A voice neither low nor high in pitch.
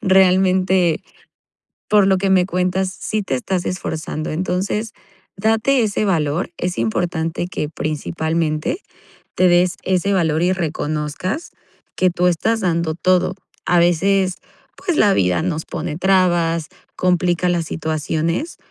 Yes: medium, 180 Hz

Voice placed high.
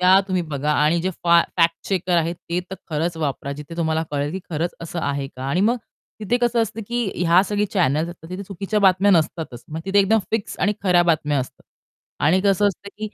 No: medium, 175 Hz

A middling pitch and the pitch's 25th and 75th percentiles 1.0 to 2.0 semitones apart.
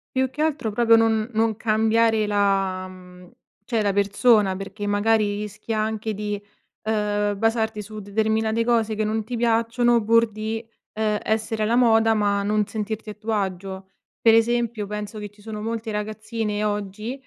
No: high, 215 Hz; narrow, 1.5 semitones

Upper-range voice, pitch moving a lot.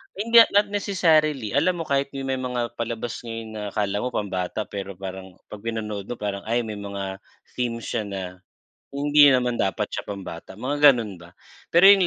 No: low, 115 Hz; wide, 5.9 semitones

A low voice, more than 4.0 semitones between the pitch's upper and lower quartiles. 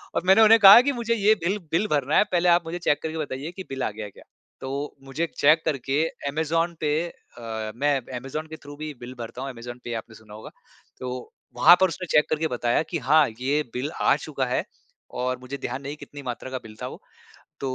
No: medium, 145 Hz; average, 4.6 semitones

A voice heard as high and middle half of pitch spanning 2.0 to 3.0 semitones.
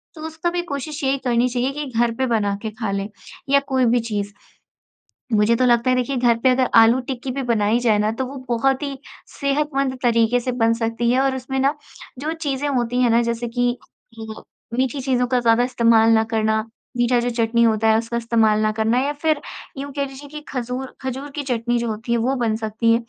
Yes: high, 245 Hz; average, 2.7 semitones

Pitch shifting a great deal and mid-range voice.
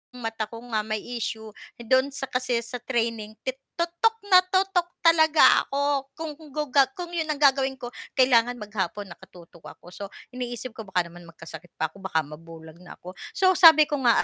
No: wide, 6.8 semitones; high, 240 Hz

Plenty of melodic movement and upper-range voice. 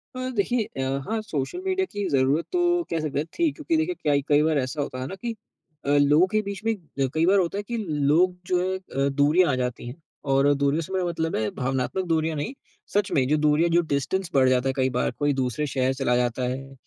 No: wide, 5.9 semitones; medium, 150 Hz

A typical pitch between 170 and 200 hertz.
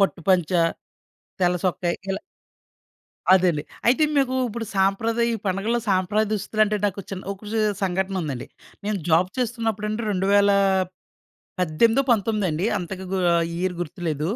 Yes: high, 195 Hz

